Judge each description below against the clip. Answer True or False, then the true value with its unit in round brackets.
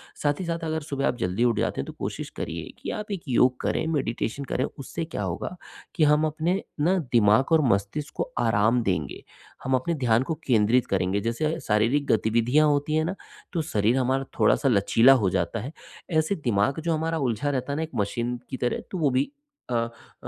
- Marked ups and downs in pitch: True (5.7 semitones)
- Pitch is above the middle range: False (130 Hz)